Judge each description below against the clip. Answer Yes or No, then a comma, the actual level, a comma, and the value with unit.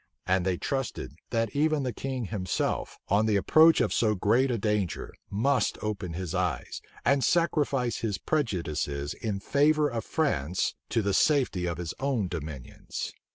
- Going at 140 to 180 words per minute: Yes, average, 155 wpm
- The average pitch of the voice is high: No, low, 105 Hz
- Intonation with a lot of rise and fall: Yes, wide, 6.9 semitones